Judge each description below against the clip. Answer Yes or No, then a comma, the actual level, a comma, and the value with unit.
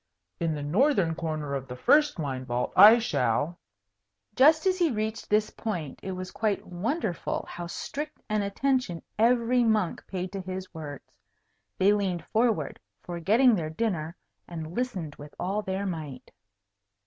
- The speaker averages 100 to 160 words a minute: Yes, average, 155 wpm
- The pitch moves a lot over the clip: Yes, wide, 6.0 semitones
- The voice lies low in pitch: No, medium, 185 Hz